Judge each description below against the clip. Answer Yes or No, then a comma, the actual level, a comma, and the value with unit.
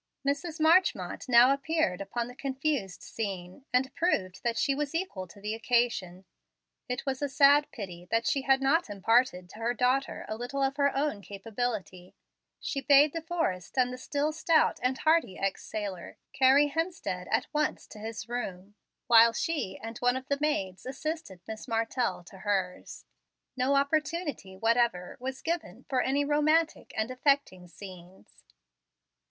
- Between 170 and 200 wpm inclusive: No, average, 160 wpm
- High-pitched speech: Yes, very high, 250 Hz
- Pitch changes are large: Yes, wide, 6.1 semitones